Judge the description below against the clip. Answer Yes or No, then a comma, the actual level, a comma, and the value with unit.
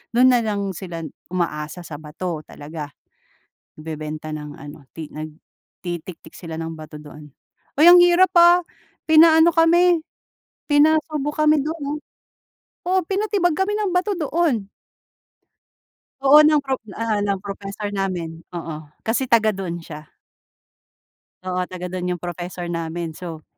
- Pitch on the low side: No, high, 195 Hz